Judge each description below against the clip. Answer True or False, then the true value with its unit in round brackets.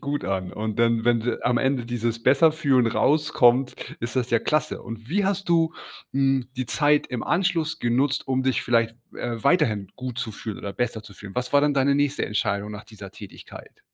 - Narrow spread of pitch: False (4.0 semitones)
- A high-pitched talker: False (125 Hz)